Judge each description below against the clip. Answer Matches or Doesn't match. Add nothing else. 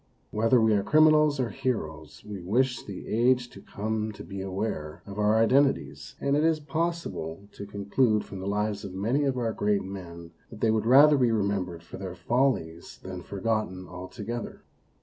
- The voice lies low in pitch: Matches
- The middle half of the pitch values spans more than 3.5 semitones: Matches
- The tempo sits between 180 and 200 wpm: Matches